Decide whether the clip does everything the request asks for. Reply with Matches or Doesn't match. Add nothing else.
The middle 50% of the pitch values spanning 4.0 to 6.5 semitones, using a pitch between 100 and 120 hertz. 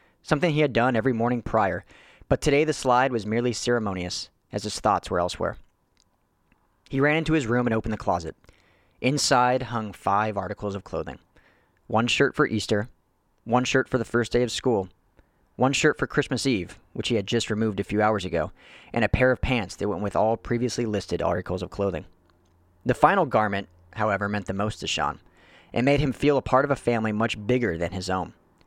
Matches